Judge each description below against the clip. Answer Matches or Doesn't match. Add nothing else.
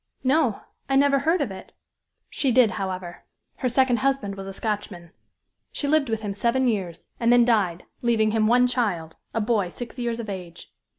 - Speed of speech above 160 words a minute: Matches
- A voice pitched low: Doesn't match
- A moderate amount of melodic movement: Matches